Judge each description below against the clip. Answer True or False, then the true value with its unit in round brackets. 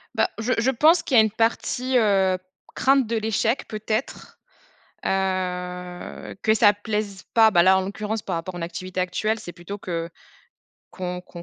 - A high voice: True (205 Hz)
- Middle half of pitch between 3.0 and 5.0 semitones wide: True (3.5 semitones)